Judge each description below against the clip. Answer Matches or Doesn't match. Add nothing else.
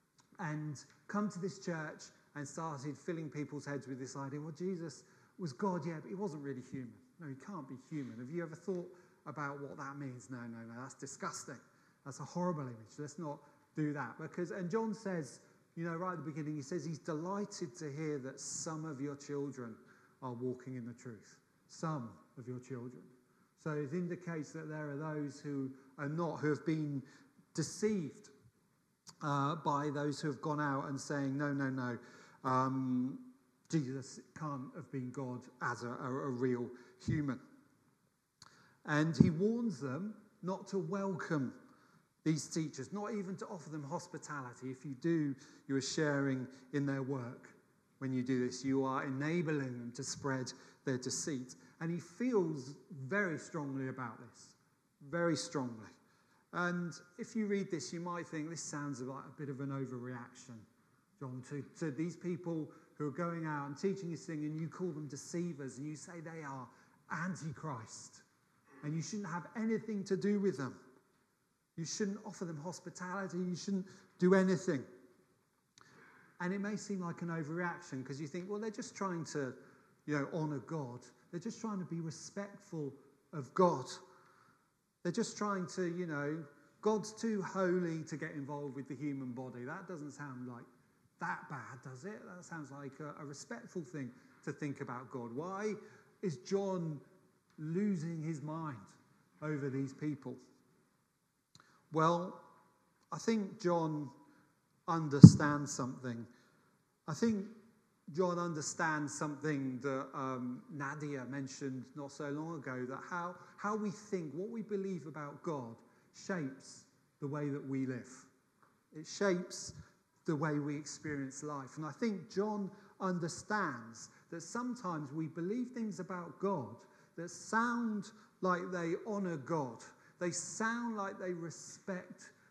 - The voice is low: Doesn't match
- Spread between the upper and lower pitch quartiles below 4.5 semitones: Doesn't match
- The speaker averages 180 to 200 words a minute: Doesn't match